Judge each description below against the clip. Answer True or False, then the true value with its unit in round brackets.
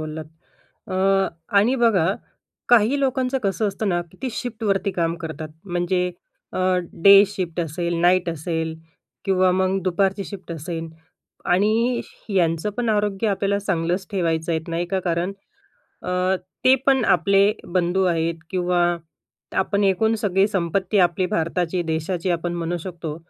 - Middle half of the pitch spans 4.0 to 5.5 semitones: False (2.9 semitones)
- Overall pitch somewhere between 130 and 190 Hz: True (185 Hz)